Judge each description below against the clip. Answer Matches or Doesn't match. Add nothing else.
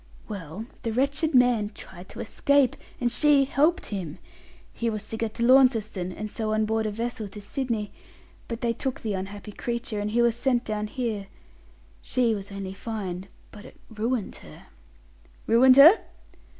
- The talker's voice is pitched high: Matches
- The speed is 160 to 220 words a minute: Matches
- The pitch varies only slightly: Doesn't match